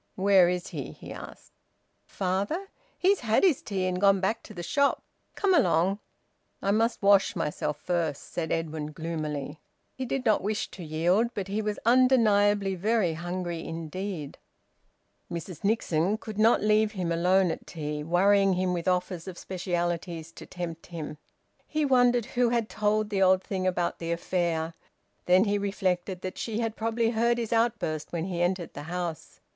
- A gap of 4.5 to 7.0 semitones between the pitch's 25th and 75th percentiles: No, average, 4.1 semitones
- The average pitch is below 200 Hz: Yes, medium, 185 Hz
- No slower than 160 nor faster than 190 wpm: Yes, average, 170 wpm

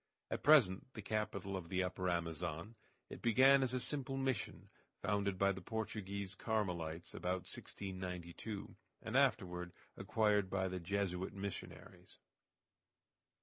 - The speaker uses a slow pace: Yes, slow, 125 wpm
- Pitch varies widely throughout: No, average, 3.3 semitones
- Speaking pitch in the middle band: No, low, 100 Hz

